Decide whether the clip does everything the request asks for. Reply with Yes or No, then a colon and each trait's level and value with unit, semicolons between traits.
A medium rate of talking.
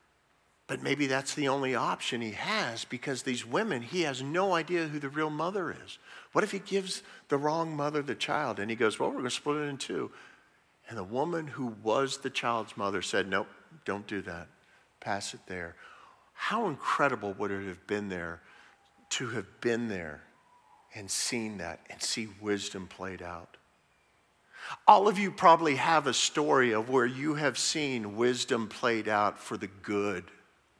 Yes: average, 180 wpm